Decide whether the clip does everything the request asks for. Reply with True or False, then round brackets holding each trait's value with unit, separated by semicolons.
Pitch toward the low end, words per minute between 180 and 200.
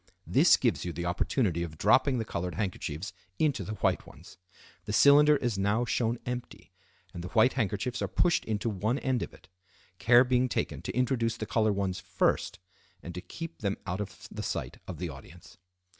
True (110 Hz; 190 wpm)